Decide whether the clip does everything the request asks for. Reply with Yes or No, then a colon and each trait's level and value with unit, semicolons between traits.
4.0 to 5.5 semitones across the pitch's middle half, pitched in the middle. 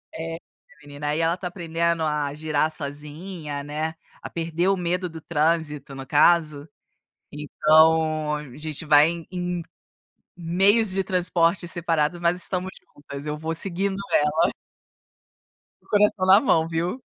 No: average, 2.8 semitones; medium, 165 Hz